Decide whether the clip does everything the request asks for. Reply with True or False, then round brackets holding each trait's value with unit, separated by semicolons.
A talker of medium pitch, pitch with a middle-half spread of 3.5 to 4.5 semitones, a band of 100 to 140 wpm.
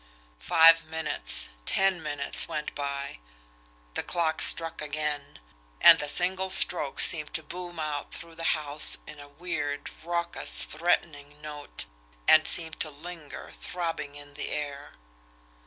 False (155 Hz; 2.4 semitones; 135 wpm)